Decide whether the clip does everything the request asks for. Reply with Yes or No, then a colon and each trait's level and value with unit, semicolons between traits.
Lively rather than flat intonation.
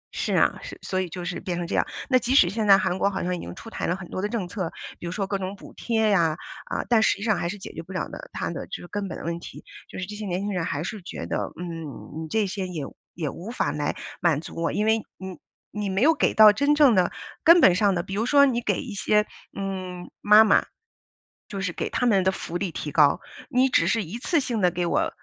No: average, 3.7 semitones